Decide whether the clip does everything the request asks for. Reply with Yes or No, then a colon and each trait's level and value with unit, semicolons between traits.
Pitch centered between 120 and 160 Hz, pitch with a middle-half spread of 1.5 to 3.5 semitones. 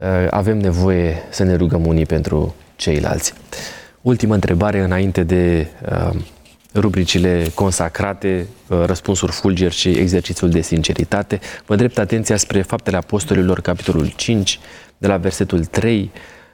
No: very low, 95 Hz; average, 3.0 semitones